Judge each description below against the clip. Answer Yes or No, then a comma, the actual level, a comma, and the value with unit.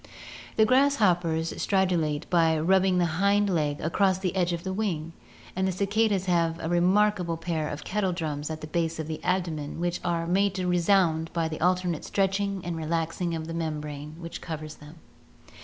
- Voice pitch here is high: No, medium, 170 Hz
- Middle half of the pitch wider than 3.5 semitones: No, average, 2.9 semitones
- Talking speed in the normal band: Yes, average, 180 wpm